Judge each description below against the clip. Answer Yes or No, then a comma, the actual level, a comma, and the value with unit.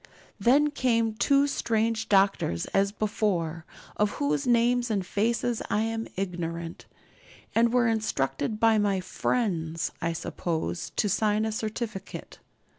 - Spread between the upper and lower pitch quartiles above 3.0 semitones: Yes, average, 4.3 semitones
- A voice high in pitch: Yes, high, 215 Hz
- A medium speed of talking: No, slow, 125 wpm